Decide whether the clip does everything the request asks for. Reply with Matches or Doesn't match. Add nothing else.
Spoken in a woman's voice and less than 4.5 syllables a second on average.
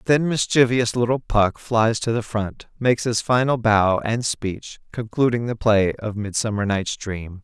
Doesn't match